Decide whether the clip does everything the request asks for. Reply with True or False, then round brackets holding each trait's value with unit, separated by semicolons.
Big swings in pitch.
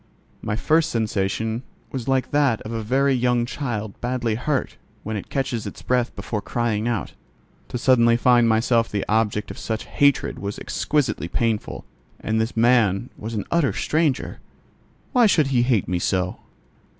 False (3.0 semitones)